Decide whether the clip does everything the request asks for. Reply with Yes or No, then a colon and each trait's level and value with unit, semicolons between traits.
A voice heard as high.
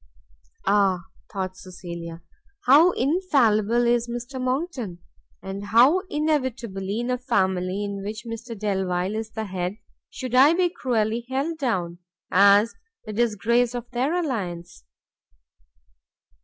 Yes: high, 225 Hz